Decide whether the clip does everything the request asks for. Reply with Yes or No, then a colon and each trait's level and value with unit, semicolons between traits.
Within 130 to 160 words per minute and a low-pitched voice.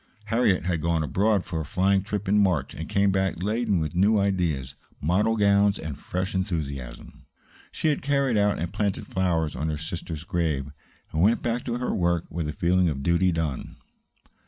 No: average, 180 wpm; very low, 90 Hz